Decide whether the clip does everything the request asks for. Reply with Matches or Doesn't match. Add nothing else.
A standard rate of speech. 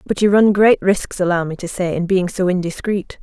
Doesn't match